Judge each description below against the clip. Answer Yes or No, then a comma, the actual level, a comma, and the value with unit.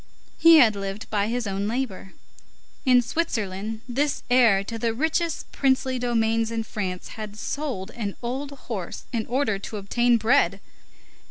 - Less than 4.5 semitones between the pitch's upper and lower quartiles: Yes, average, 4.0 semitones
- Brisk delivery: No, average, 150 wpm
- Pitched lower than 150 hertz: No, high, 230 Hz